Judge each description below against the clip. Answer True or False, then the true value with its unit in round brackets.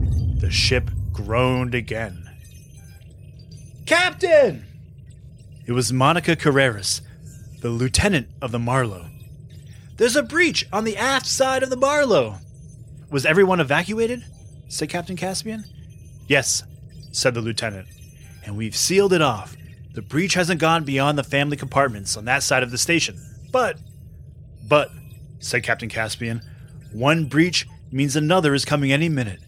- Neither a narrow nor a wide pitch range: False (5.9 semitones)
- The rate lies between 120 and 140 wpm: True (135 wpm)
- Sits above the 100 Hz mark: True (135 Hz)